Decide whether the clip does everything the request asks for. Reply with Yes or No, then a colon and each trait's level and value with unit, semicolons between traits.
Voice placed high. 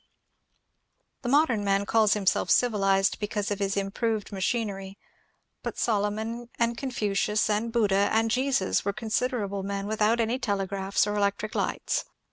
Yes: high, 210 Hz